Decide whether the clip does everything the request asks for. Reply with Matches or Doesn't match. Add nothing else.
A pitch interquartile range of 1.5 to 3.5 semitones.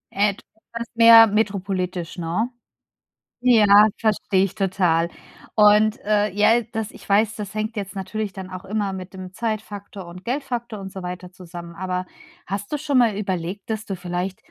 Matches